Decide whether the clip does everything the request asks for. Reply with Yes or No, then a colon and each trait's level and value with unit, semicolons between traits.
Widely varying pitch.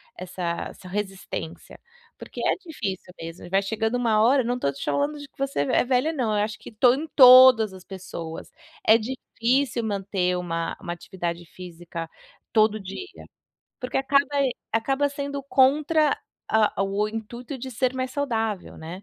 Yes: wide, 5.9 semitones